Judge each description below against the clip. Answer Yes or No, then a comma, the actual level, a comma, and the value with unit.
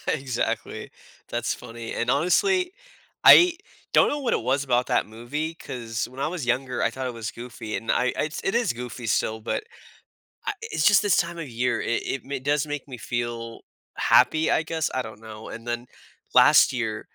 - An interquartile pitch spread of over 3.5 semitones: Yes, average, 5.1 semitones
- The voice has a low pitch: Yes, low, 125 Hz